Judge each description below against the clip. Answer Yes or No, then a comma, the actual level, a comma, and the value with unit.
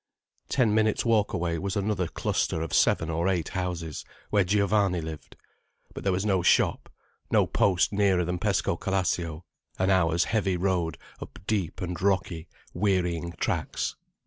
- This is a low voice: Yes, very low, 90 Hz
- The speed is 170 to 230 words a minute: No, average, 145 wpm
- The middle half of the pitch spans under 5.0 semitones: Yes, average, 2.8 semitones